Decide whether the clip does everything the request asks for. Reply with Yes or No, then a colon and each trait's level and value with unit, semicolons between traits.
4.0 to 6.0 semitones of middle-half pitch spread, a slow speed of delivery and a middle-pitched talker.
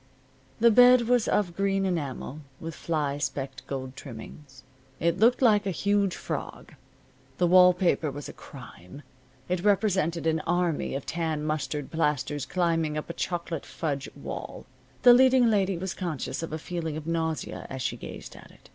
No: average, 4.4 semitones; average, 165 wpm; medium, 165 Hz